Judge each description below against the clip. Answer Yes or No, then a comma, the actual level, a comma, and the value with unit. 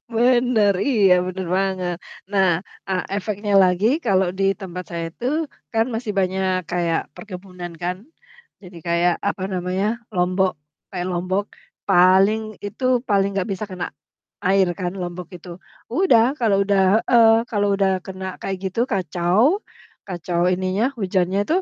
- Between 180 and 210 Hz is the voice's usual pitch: Yes, high, 190 Hz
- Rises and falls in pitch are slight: Yes, narrow, 2.2 semitones